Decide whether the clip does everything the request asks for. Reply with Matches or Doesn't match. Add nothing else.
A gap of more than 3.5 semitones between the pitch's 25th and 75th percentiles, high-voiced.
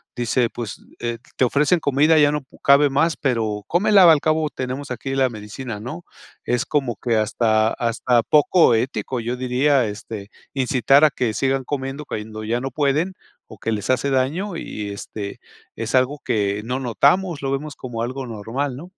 Doesn't match